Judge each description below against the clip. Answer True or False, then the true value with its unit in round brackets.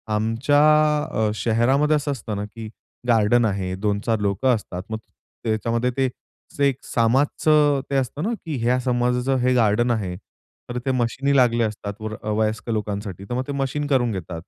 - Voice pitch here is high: False (120 Hz)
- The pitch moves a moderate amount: True (3.6 semitones)